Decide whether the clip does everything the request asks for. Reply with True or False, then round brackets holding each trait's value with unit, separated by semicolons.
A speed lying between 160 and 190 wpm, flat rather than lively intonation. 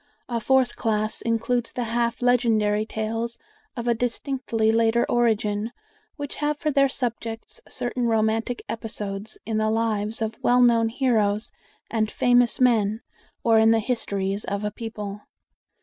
False (145 wpm; 2.0 semitones)